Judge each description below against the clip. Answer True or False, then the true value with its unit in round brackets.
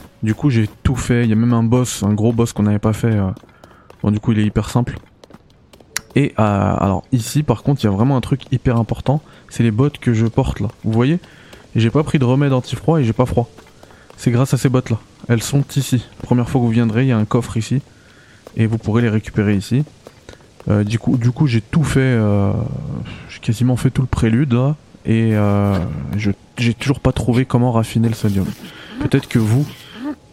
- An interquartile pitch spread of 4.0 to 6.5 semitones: False (3.3 semitones)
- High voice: False (120 Hz)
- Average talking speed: False (230 wpm)